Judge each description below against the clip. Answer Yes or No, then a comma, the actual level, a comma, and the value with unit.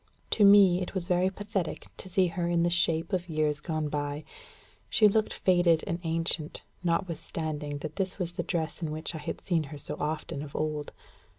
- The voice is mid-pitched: Yes, medium, 165 Hz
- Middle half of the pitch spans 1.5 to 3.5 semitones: Yes, average, 2.8 semitones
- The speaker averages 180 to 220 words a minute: Yes, average, 195 wpm